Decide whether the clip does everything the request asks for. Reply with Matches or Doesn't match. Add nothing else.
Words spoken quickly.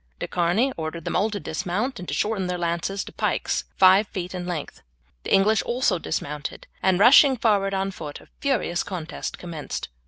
Doesn't match